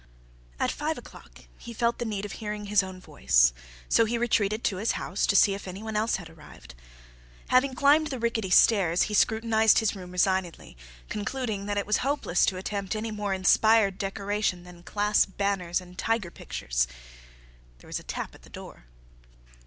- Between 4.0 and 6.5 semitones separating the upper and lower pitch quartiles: No, average, 3.2 semitones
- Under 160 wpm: No, average, 185 wpm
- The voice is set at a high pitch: Yes, high, 205 Hz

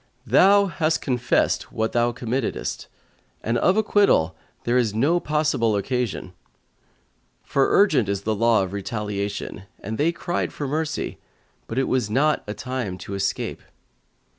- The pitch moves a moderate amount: No, wide, 6.3 semitones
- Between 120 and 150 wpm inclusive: Yes, average, 140 wpm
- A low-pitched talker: Yes, low, 120 Hz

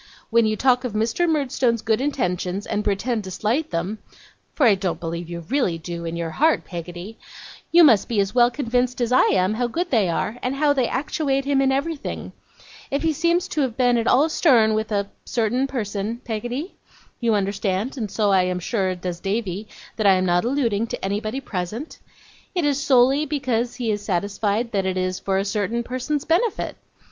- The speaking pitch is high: Yes, high, 225 Hz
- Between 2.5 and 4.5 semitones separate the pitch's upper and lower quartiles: No, average, 5.3 semitones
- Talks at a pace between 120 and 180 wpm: No, average, 200 wpm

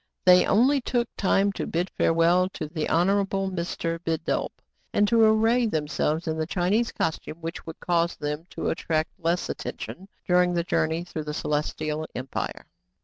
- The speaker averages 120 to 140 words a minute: No, average, 165 wpm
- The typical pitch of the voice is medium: Yes, medium, 170 Hz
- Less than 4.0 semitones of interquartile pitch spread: Yes, average, 3.5 semitones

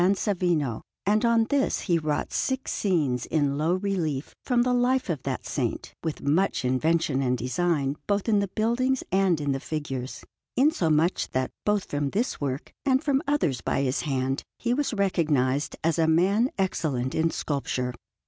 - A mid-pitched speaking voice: Yes, medium, 165 Hz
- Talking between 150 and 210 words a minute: Yes, average, 165 wpm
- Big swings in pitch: Yes, wide, 7.0 semitones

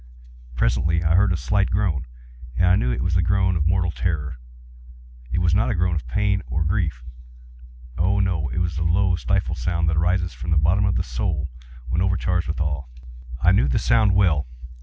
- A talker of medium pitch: No, very low, 85 Hz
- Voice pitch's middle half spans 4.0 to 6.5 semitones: Yes, average, 4.5 semitones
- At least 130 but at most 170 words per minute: No, average, 200 wpm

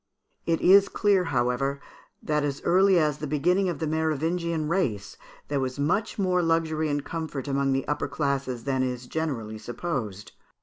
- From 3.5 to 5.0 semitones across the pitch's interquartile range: Yes, average, 3.8 semitones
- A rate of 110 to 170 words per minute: Yes, average, 165 wpm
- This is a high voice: No, medium, 150 Hz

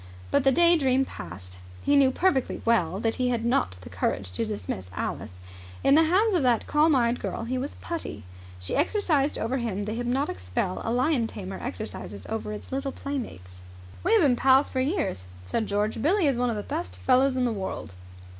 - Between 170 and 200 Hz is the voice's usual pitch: No, high, 245 Hz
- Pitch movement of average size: No, wide, 6.3 semitones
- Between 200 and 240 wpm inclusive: Yes, fast, 205 wpm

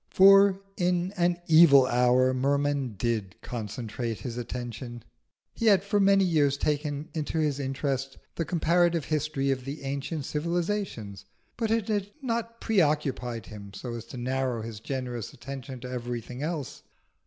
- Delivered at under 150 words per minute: Yes, average, 140 wpm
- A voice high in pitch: No, medium, 140 Hz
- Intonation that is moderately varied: No, wide, 5.9 semitones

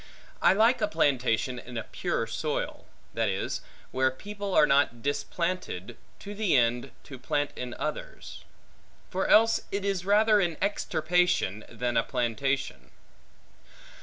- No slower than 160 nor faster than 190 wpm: No, slow, 135 wpm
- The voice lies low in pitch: No, medium, 150 Hz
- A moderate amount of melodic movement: No, wide, 8.1 semitones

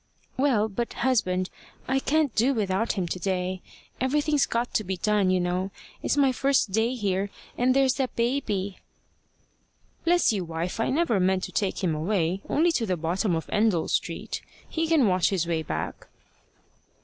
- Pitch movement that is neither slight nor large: No, wide, 5.9 semitones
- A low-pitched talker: No, high, 210 Hz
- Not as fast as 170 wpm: No, average, 175 wpm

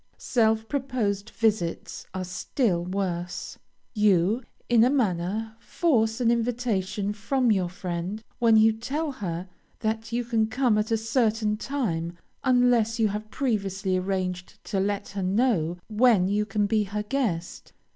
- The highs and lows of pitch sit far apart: No, average, 3.5 semitones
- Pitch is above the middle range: Yes, high, 215 Hz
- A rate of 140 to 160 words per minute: Yes, average, 145 wpm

